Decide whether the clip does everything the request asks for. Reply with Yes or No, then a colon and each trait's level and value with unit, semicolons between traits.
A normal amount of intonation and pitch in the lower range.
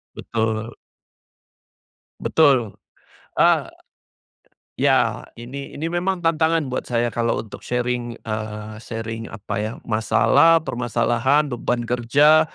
Yes: average, 4.5 semitones; low, 120 Hz